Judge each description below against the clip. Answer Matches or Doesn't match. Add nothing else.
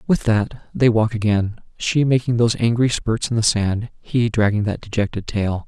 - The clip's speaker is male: Matches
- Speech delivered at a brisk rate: Doesn't match